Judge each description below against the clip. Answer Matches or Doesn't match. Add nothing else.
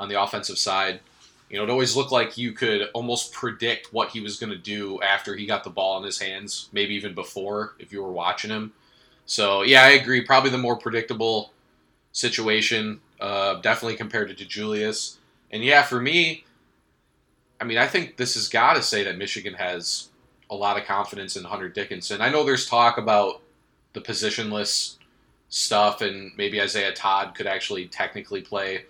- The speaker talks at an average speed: Matches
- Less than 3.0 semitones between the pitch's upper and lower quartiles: Doesn't match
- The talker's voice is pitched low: Matches